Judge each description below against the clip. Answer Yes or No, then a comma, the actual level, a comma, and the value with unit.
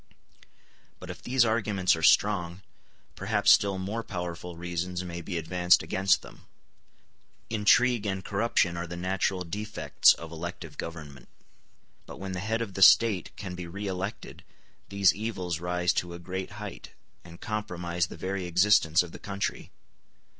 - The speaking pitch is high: No, very low, 90 Hz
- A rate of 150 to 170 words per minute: Yes, average, 155 wpm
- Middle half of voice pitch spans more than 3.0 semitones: No, average, 2.7 semitones